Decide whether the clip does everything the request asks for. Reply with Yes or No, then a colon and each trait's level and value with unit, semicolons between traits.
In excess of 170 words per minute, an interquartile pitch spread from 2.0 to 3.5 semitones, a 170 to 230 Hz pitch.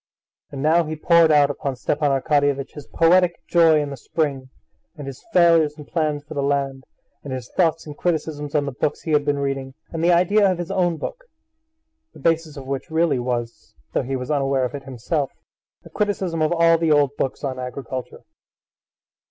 No: average, 195 wpm; average, 3.2 semitones; medium, 150 Hz